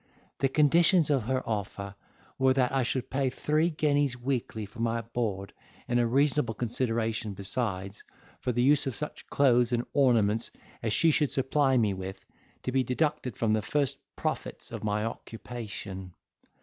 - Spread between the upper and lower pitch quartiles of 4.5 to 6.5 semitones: No, average, 3.9 semitones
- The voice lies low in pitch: Yes, low, 120 Hz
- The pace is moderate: Yes, average, 160 wpm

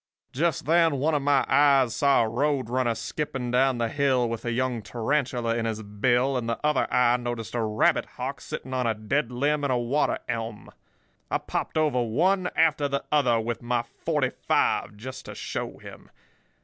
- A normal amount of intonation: Yes, average, 3.4 semitones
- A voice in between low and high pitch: No, low, 125 Hz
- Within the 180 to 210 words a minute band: Yes, average, 190 wpm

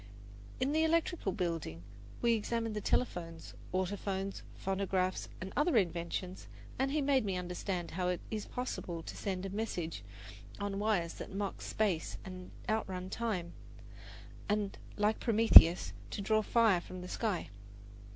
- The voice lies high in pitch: Yes, high, 195 Hz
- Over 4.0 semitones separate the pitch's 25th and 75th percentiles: No, average, 3.4 semitones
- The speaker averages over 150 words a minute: No, average, 140 wpm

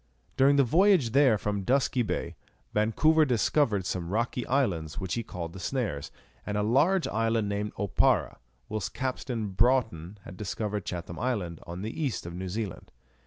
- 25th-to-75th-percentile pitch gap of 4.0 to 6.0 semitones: Yes, wide, 5.5 semitones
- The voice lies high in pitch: No, low, 110 Hz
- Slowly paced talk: No, average, 165 wpm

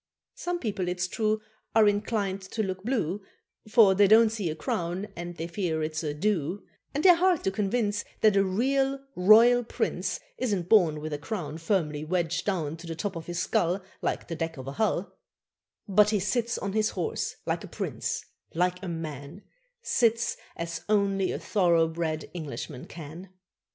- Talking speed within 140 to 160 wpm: No, average, 175 wpm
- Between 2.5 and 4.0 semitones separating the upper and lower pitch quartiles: No, average, 4.4 semitones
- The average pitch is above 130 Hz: Yes, high, 190 Hz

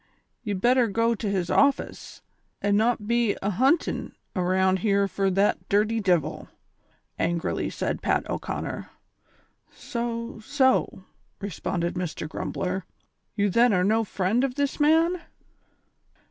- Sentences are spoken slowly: Yes, slow, 125 wpm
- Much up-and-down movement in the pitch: No, average, 4.1 semitones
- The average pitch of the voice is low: No, high, 205 Hz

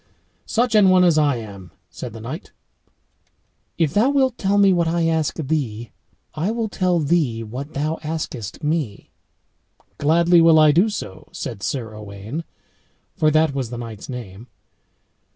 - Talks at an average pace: Yes, average, 155 wpm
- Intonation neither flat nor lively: No, wide, 6.6 semitones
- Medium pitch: Yes, medium, 155 Hz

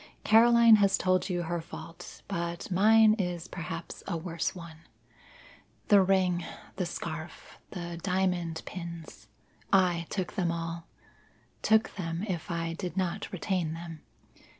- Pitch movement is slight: Yes, narrow, 2.3 semitones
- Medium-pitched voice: Yes, medium, 175 Hz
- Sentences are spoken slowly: Yes, slow, 130 wpm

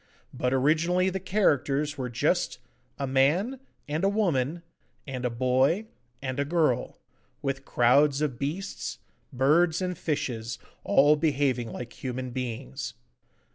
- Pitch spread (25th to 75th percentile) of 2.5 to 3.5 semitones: No, average, 4.4 semitones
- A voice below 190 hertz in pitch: Yes, medium, 140 Hz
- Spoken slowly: Yes, slow, 130 wpm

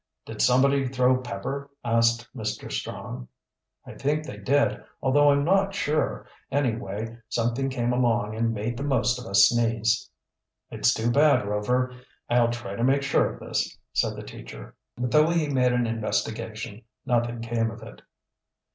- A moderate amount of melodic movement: Yes, average, 3.0 semitones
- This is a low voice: Yes, low, 120 Hz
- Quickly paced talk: No, average, 160 wpm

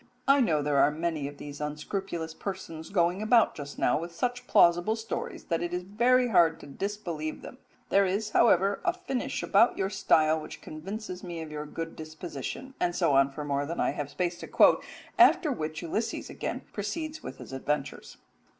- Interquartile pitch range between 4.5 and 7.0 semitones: Yes, average, 5.3 semitones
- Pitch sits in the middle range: Yes, medium, 170 Hz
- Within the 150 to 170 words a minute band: No, average, 190 wpm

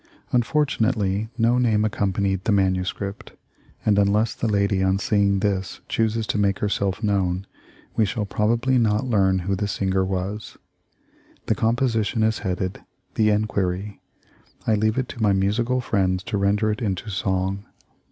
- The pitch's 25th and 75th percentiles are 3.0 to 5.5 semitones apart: No, narrow, 2.4 semitones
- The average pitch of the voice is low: Yes, low, 105 Hz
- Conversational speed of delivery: Yes, average, 150 wpm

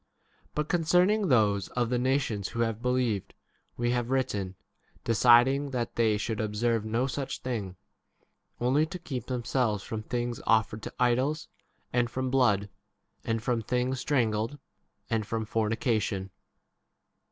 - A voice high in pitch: No, low, 120 Hz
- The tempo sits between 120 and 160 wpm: Yes, average, 140 wpm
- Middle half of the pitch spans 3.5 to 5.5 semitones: No, average, 3.0 semitones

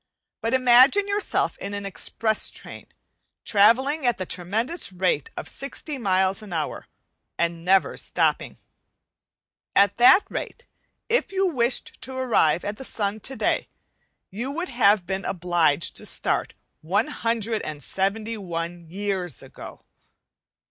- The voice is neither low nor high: No, high, 205 Hz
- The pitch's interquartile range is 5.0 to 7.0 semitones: Yes, average, 5.3 semitones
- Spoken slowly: Yes, slow, 120 wpm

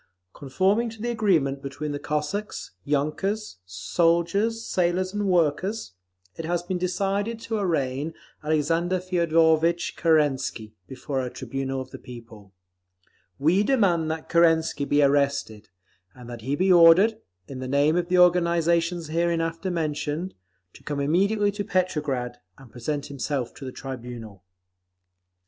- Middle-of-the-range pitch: Yes, medium, 165 Hz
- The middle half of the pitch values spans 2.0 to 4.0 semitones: No, average, 4.8 semitones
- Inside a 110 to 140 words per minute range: Yes, slow, 135 wpm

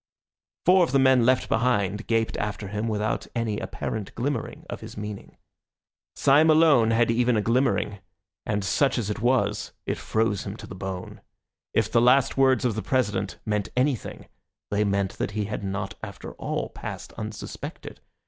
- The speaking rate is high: No, average, 170 wpm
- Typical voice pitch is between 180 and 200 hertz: No, low, 110 Hz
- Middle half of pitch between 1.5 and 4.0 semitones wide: Yes, average, 3.6 semitones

